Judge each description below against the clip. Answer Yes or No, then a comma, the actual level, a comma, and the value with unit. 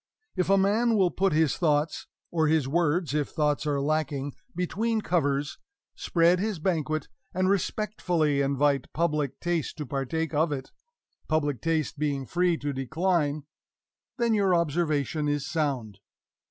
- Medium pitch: Yes, medium, 155 Hz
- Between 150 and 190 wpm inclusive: No, average, 140 wpm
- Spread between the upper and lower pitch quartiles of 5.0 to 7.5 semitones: No, average, 3.5 semitones